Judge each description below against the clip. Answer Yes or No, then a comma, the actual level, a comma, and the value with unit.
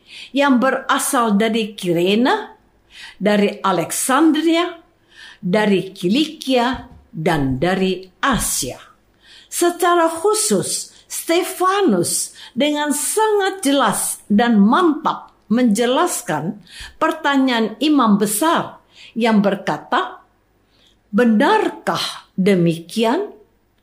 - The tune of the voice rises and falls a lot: Yes, wide, 8.1 semitones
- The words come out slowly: Yes, slow, 70 wpm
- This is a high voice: Yes, very high, 255 Hz